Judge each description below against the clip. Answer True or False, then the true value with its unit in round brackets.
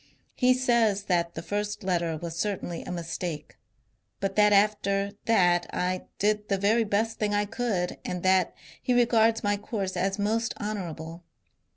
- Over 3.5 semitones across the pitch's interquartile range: False (3.1 semitones)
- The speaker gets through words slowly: False (160 wpm)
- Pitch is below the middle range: False (200 Hz)